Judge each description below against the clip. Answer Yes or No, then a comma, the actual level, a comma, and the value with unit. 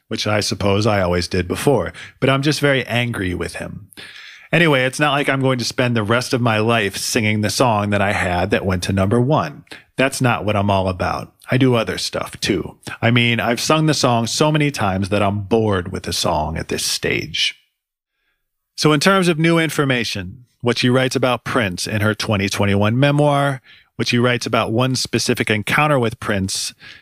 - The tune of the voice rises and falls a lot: No, average, 4.7 semitones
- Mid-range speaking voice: No, low, 115 Hz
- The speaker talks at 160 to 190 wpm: No, average, 200 wpm